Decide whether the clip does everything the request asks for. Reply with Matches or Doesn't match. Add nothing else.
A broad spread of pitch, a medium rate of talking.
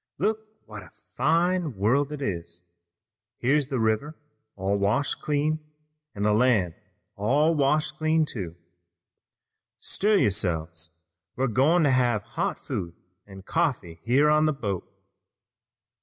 Doesn't match